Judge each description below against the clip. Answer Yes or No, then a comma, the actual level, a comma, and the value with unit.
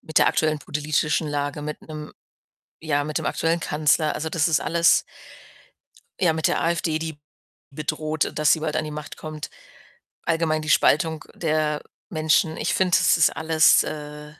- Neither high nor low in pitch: Yes, medium, 155 Hz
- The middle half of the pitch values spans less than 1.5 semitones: Yes, narrow, 1.0 semitones